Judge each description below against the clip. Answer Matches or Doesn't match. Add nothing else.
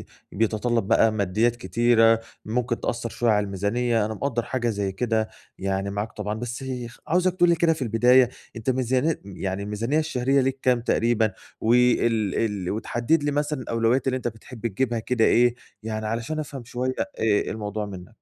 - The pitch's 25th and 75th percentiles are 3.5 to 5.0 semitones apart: Doesn't match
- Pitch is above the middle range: Doesn't match